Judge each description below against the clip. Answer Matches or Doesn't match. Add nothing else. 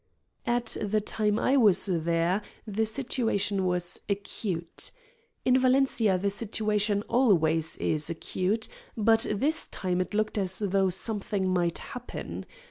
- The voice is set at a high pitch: Matches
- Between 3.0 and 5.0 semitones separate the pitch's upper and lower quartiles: Matches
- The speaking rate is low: Matches